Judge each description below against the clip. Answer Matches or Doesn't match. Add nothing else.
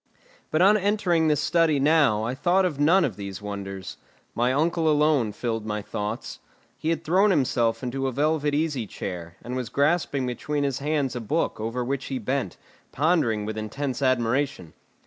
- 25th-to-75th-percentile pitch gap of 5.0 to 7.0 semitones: Matches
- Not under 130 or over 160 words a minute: Doesn't match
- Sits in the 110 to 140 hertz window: Matches